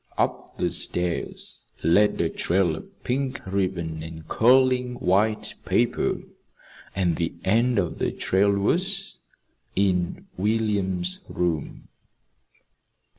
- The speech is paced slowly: Yes, slow, 105 wpm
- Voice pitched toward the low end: Yes, very low, 95 Hz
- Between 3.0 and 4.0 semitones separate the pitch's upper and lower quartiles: No, average, 4.4 semitones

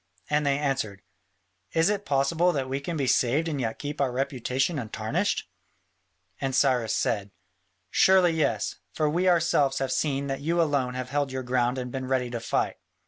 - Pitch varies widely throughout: No, average, 3.1 semitones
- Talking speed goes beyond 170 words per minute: Yes, average, 180 wpm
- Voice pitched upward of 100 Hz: Yes, low, 135 Hz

